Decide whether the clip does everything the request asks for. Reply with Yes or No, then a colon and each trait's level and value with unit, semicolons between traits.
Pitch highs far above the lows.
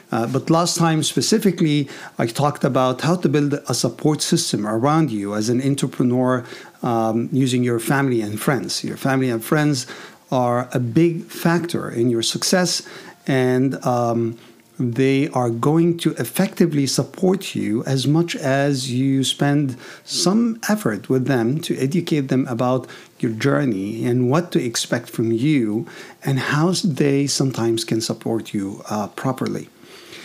No: average, 4.9 semitones